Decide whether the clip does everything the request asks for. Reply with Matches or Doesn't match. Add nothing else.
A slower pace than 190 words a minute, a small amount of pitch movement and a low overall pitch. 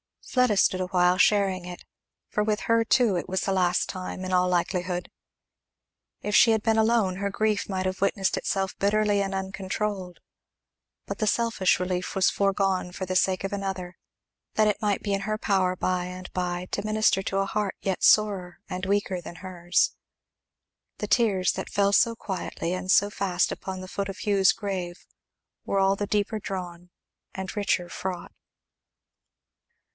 Doesn't match